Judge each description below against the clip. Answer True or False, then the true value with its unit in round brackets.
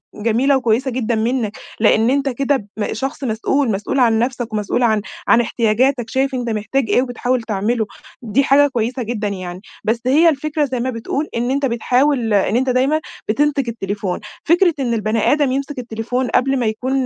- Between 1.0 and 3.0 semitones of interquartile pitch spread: False (3.5 semitones)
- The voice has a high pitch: True (245 Hz)